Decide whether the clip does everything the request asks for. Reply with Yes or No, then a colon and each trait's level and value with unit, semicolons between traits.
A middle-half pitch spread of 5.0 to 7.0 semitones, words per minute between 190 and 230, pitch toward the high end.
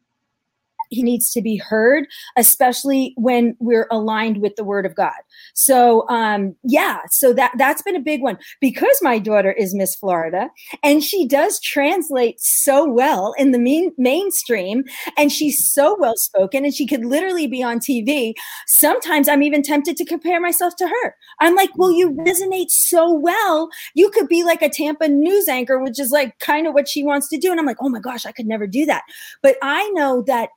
Yes: wide, 5.6 semitones; average, 200 wpm; very high, 285 Hz